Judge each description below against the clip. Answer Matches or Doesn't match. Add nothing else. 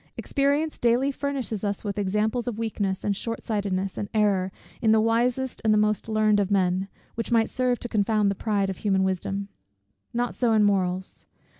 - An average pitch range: Matches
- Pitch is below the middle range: Doesn't match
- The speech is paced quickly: Doesn't match